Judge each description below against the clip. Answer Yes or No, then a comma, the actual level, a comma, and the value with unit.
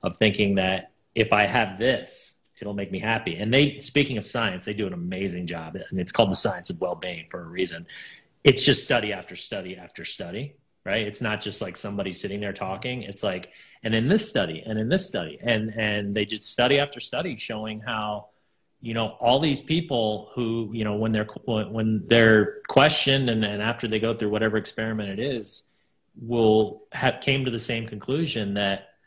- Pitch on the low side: Yes, low, 110 Hz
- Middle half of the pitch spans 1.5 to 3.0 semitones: Yes, narrow, 2.6 semitones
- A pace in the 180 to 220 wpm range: Yes, fast, 205 wpm